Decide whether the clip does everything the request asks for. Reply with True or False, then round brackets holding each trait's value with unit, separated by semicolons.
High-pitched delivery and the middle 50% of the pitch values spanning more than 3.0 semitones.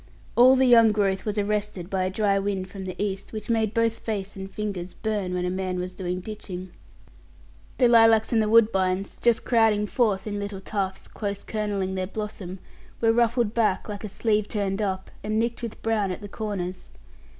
False (205 Hz; 2.6 semitones)